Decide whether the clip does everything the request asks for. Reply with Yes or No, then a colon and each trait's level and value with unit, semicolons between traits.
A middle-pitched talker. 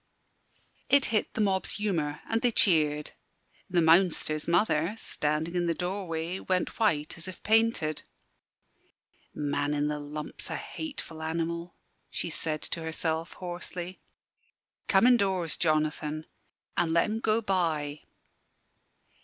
Yes: medium, 170 Hz